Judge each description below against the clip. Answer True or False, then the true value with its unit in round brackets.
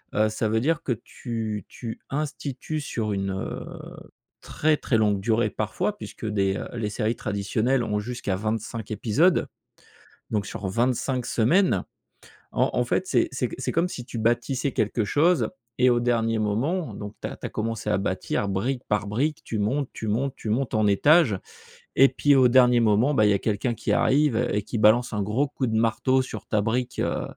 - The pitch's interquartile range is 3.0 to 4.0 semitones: True (3.7 semitones)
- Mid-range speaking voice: False (115 Hz)